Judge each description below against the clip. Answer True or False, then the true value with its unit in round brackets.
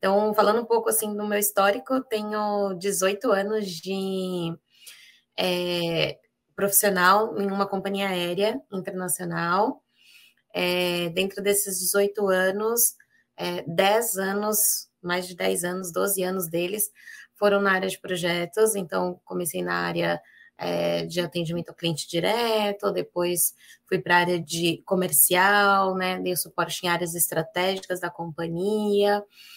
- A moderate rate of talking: True (130 wpm)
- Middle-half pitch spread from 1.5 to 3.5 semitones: True (2.8 semitones)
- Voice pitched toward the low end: False (190 Hz)